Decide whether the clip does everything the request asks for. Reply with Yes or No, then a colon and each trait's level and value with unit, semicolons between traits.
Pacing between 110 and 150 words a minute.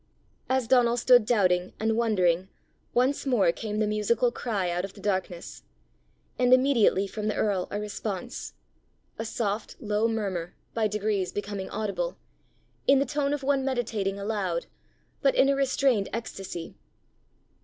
Yes: average, 145 wpm